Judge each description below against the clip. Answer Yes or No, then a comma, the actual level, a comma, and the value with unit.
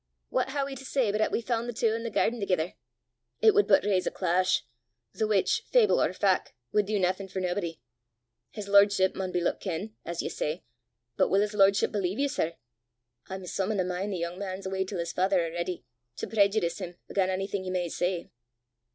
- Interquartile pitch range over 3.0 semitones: No, average, 2.7 semitones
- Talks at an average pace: No, fast, 220 wpm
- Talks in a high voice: Yes, high, 195 Hz